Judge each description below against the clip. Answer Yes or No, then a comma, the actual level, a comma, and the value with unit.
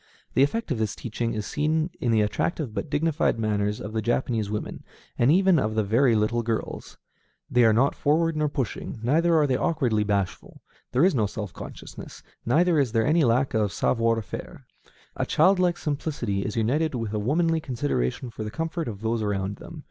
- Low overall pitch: Yes, low, 120 Hz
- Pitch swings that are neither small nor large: No, wide, 6.1 semitones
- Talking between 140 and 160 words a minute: No, average, 195 wpm